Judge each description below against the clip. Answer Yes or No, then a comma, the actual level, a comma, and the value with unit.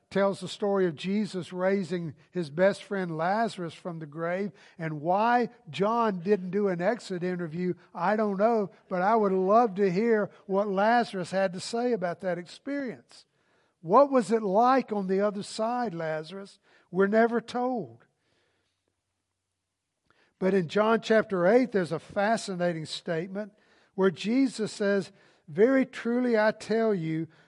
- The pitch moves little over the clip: No, average, 3.7 semitones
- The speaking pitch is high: Yes, high, 195 Hz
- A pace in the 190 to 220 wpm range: No, average, 145 wpm